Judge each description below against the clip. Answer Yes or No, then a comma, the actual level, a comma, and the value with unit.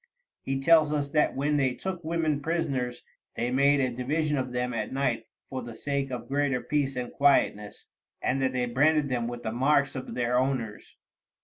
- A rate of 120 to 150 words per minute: No, average, 190 wpm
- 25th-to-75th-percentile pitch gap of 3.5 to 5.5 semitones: No, average, 2.7 semitones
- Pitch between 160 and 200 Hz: No, low, 135 Hz